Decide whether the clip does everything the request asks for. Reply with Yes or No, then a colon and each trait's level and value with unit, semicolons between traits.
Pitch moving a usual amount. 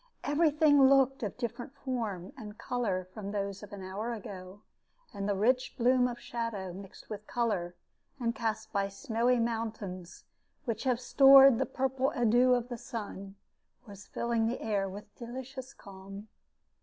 Yes: average, 3.9 semitones